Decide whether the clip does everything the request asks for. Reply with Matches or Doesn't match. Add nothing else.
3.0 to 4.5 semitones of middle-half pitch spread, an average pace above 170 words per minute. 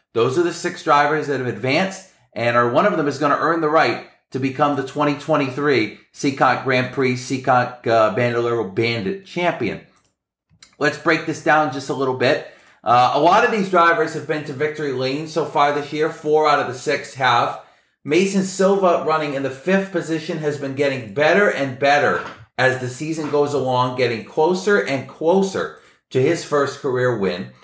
Matches